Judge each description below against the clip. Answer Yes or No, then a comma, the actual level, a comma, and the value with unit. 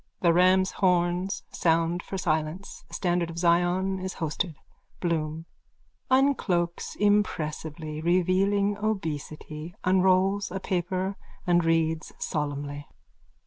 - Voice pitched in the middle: Yes, medium, 175 Hz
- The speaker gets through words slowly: Yes, slow, 105 wpm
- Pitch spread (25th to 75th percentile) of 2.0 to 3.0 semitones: Yes, average, 2.7 semitones